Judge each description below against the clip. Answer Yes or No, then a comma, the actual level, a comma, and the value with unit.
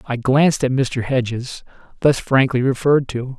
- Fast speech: No, average, 160 wpm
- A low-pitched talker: Yes, low, 130 Hz